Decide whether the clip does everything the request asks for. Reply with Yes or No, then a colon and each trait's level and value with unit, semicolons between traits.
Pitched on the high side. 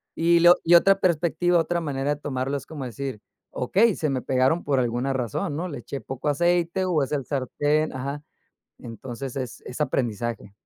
No: medium, 140 Hz